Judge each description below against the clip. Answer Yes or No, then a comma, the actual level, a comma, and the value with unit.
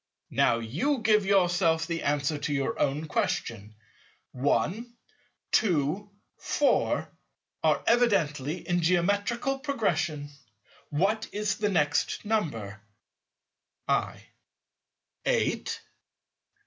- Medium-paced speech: No, slow, 95 wpm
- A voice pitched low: No, medium, 175 Hz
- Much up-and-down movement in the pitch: Yes, wide, 6.4 semitones